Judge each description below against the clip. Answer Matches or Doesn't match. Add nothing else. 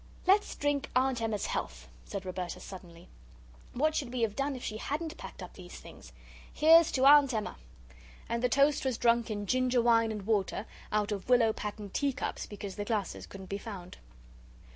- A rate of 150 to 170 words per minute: Doesn't match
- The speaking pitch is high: Matches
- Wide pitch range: Doesn't match